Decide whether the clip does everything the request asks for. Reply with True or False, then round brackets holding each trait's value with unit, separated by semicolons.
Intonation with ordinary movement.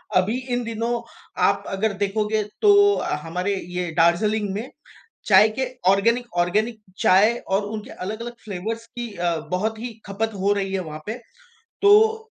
True (3.4 semitones)